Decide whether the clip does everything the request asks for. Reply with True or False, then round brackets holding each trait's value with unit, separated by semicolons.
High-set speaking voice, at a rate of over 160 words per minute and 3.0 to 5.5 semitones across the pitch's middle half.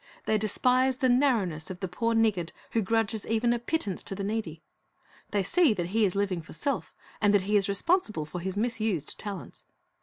True (210 Hz; 200 wpm; 3.5 semitones)